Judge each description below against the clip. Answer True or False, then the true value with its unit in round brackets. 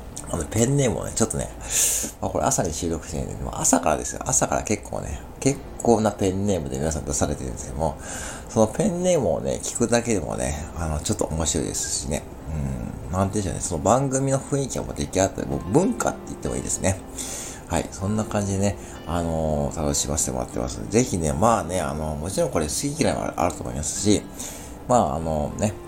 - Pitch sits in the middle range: False (85 Hz)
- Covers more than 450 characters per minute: True (460 characters per minute)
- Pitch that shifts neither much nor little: False (6.4 semitones)